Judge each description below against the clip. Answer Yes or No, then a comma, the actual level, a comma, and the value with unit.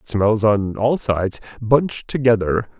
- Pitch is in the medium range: No, low, 110 Hz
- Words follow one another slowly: Yes, slow, 130 wpm